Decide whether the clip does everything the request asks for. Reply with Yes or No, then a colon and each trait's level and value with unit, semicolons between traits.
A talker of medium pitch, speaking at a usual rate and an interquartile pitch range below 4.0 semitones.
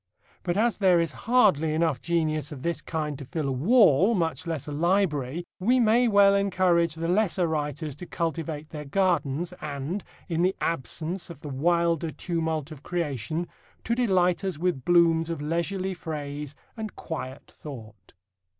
Yes: medium, 165 Hz; average, 160 wpm; average, 3.5 semitones